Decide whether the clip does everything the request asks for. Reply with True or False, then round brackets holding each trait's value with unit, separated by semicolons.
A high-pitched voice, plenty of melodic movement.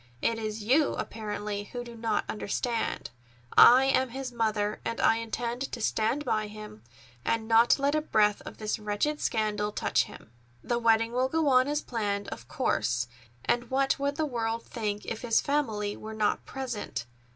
False (225 Hz; 3.3 semitones)